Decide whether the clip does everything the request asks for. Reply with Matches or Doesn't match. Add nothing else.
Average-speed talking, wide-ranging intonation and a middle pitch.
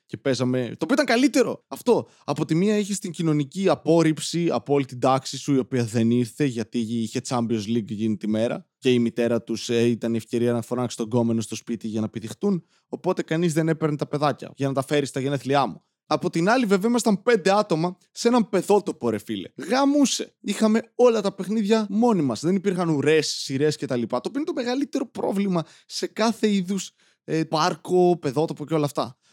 Doesn't match